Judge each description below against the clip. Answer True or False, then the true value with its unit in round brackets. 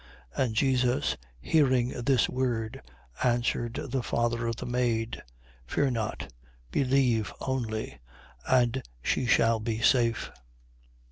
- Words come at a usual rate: False (115 wpm)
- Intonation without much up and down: True (2.1 semitones)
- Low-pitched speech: True (120 Hz)